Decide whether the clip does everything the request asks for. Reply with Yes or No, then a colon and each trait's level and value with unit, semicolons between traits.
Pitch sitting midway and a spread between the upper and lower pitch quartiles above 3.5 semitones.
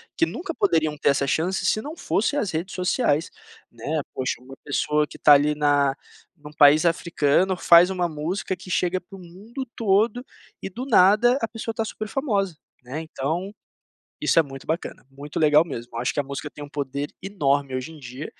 Yes: medium, 160 Hz; average, 5.2 semitones